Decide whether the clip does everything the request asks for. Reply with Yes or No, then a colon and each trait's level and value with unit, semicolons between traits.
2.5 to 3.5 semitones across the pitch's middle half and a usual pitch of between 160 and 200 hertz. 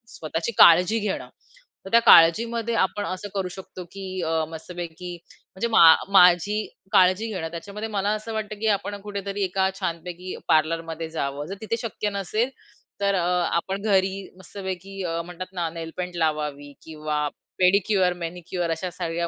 Yes: average, 3.2 semitones; medium, 185 Hz